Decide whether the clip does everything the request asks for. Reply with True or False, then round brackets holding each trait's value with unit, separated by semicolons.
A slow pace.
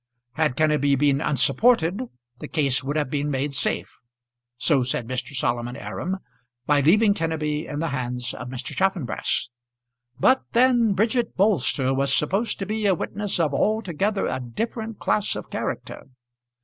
False (150 wpm)